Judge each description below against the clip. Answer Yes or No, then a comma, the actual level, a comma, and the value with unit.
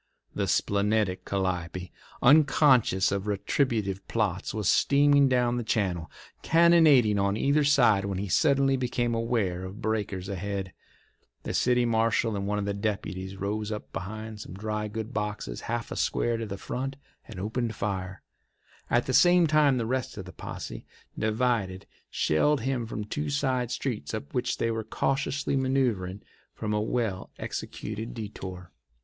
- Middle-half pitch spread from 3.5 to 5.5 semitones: Yes, average, 4.1 semitones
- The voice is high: No, low, 110 Hz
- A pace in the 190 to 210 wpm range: No, average, 155 wpm